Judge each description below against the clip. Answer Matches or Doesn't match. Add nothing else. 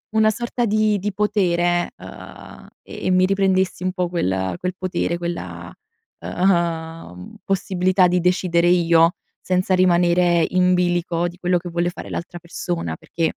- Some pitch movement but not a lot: Doesn't match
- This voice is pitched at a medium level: Matches